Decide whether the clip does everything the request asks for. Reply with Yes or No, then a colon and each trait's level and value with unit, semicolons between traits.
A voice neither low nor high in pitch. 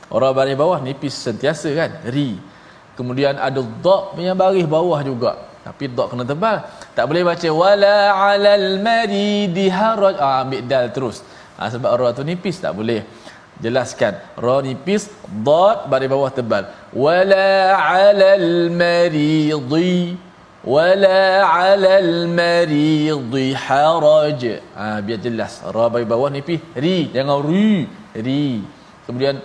Yes: medium, 165 Hz